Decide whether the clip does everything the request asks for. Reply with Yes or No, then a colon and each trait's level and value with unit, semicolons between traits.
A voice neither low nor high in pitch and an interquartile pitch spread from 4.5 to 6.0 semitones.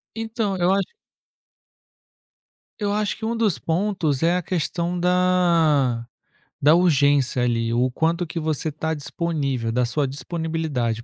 Yes: medium, 160 Hz; average, 5.1 semitones